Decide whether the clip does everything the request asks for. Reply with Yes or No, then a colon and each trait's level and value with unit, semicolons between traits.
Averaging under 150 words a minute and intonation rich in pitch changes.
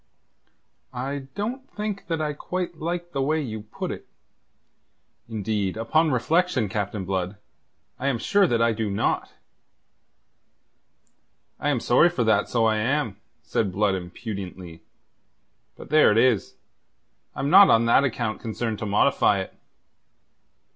Yes: average, 140 wpm; wide, 6.7 semitones